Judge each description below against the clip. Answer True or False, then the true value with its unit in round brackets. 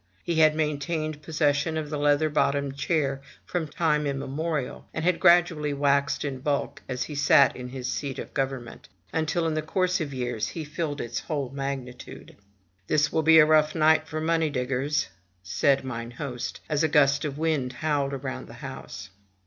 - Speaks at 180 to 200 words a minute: True (185 wpm)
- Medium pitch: True (145 Hz)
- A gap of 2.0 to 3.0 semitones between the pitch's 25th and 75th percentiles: True (2.5 semitones)